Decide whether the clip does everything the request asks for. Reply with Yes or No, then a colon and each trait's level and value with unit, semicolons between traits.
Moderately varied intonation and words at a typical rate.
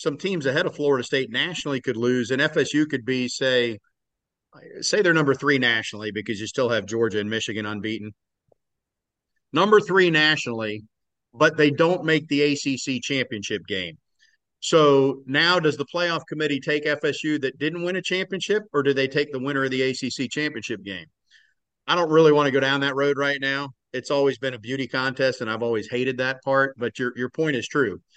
Yes: average, 3.5 semitones; average, 195 wpm